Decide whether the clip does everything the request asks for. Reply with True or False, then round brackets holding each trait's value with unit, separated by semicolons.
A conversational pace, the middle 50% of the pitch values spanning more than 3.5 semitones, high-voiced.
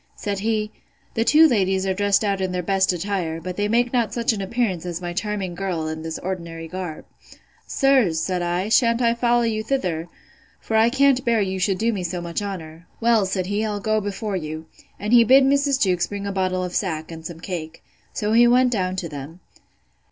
False (215 wpm; 4.3 semitones; 195 Hz)